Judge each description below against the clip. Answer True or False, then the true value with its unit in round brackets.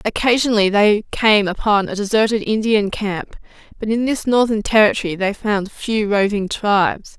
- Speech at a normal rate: True (150 wpm)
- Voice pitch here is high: True (210 Hz)